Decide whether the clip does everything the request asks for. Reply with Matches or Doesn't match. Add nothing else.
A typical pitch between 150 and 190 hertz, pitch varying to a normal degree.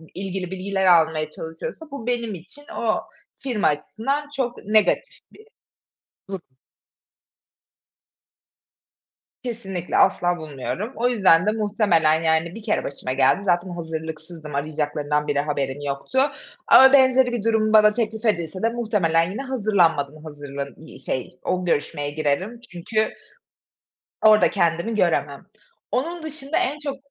Doesn't match